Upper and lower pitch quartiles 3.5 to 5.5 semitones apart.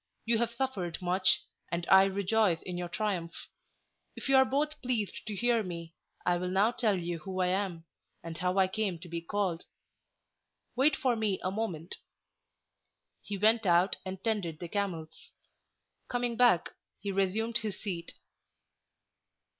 Yes: average, 4.1 semitones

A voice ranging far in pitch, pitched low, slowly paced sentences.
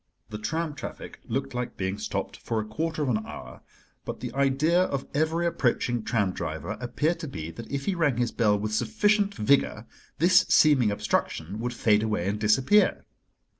No: wide, 6.7 semitones; low, 125 Hz; average, 180 wpm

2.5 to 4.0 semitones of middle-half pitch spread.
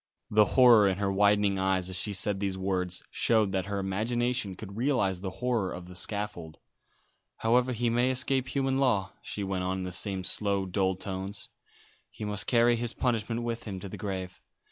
Yes: average, 3.7 semitones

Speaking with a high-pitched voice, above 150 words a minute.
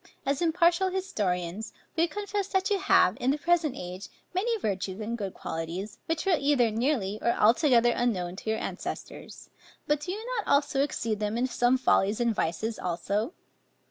Yes: high, 240 Hz; average, 170 wpm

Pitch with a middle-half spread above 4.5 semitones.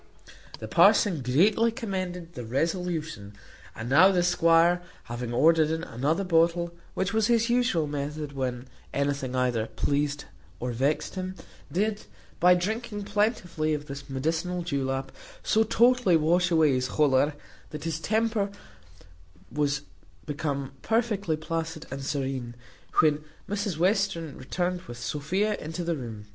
Yes: average, 4.9 semitones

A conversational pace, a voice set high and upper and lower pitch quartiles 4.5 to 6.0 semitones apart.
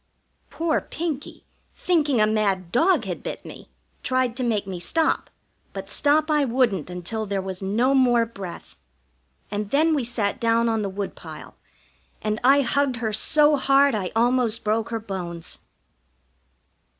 Yes: average, 150 wpm; high, 230 Hz; average, 5.2 semitones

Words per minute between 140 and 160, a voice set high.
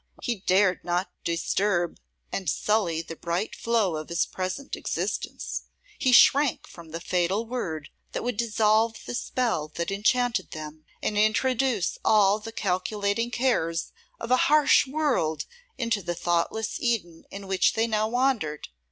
Yes: average, 145 wpm; high, 205 Hz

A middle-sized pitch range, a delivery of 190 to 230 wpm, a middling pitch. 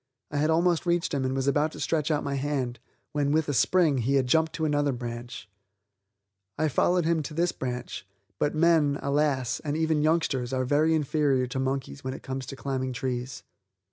Yes: average, 3.1 semitones; average, 200 wpm; medium, 145 Hz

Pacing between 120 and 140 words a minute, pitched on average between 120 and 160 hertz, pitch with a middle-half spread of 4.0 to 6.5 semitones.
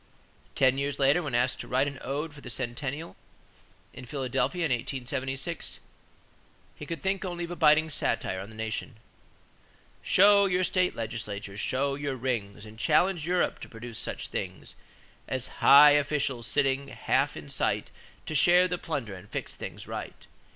No: average, 165 wpm; low, 135 Hz; average, 4.7 semitones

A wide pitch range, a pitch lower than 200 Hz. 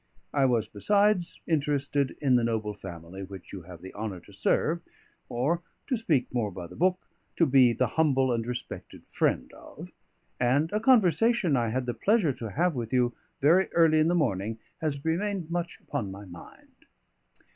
Yes: wide, 7.1 semitones; low, 135 Hz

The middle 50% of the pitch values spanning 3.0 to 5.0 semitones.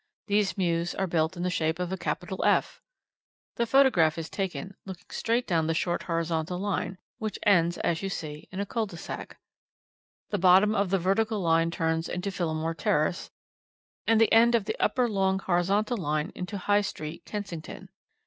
Yes: average, 3.5 semitones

